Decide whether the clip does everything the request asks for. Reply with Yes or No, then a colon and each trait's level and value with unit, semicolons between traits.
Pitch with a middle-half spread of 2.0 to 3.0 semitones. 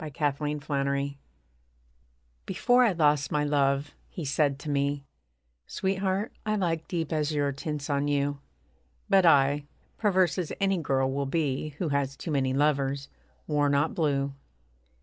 Yes: average, 2.7 semitones